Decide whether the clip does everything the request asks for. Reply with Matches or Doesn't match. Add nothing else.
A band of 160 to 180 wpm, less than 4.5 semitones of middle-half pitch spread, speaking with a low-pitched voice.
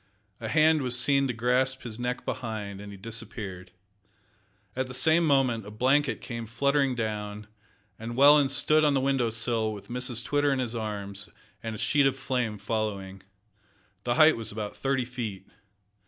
Matches